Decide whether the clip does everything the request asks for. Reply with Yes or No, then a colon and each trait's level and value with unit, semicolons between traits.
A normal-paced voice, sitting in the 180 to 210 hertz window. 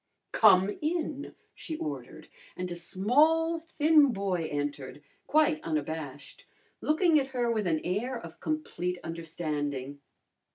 No: slow, 120 wpm; medium, 185 Hz